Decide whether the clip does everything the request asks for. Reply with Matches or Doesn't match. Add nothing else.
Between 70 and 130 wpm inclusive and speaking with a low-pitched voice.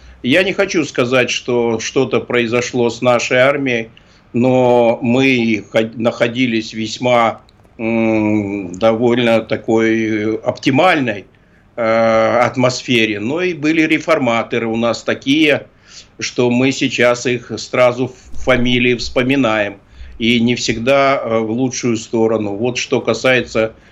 Matches